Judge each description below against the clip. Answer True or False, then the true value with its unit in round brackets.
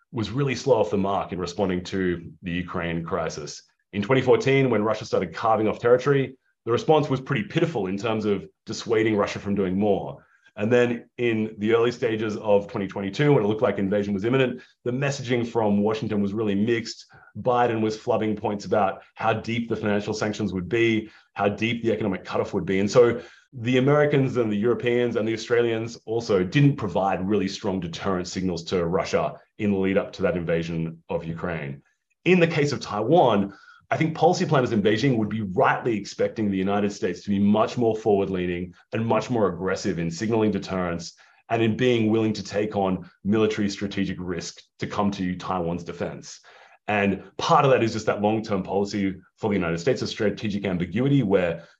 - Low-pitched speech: True (105 Hz)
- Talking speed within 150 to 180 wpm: False (190 wpm)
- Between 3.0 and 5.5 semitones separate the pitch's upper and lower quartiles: True (3.3 semitones)